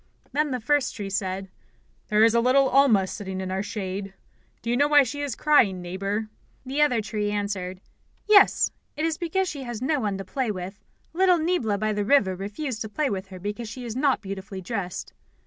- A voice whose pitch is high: Yes, high, 215 Hz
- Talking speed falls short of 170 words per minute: No, average, 200 wpm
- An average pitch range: No, wide, 6.1 semitones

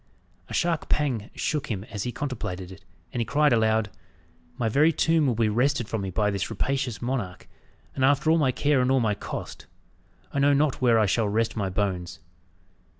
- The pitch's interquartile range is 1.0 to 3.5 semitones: No, average, 5.1 semitones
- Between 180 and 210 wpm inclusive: Yes, average, 200 wpm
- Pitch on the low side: Yes, low, 120 Hz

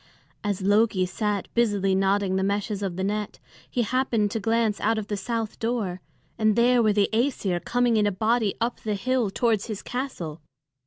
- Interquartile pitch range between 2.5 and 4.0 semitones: Yes, average, 2.9 semitones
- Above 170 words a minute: Yes, average, 190 wpm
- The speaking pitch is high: Yes, high, 210 Hz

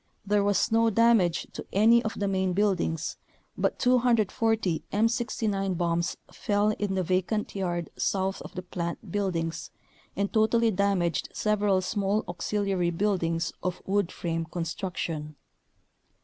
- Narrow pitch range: No, average, 3.4 semitones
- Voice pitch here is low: No, high, 195 Hz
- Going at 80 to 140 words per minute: Yes, slow, 135 wpm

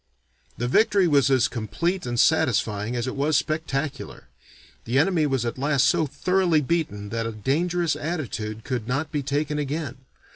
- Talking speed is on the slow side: No, average, 170 wpm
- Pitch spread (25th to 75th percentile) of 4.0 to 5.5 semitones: Yes, average, 4.7 semitones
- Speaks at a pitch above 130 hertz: Yes, medium, 140 Hz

